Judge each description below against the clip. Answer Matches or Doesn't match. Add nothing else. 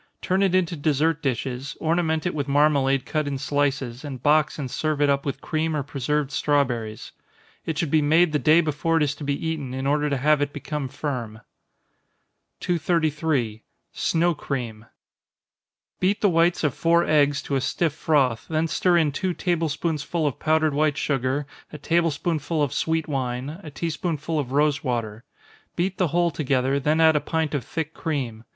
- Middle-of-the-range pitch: Matches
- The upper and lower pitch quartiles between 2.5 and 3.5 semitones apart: Matches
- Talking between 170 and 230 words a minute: Matches